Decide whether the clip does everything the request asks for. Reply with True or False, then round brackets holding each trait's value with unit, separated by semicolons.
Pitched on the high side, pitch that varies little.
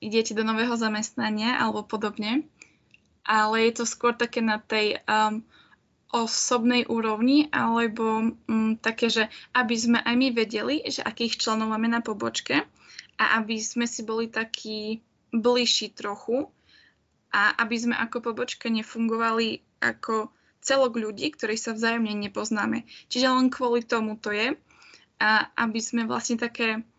True (230 Hz; 1.5 semitones)